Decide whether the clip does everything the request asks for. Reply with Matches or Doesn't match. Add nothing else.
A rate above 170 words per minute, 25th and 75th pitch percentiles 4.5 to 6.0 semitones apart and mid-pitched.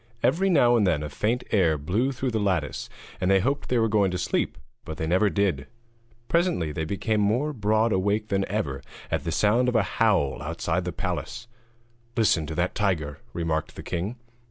Doesn't match